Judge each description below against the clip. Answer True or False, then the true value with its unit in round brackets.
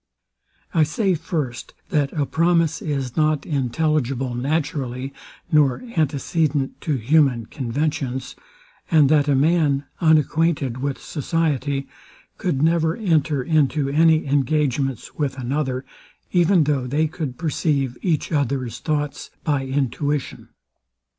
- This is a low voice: False (145 Hz)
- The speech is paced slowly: True (115 wpm)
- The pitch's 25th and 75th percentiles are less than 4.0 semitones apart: True (2.9 semitones)